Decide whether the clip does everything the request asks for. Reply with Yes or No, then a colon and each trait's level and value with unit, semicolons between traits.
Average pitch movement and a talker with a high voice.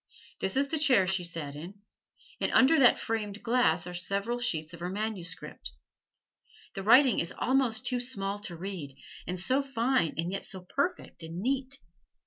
No: wide, 6.3 semitones; high, 200 Hz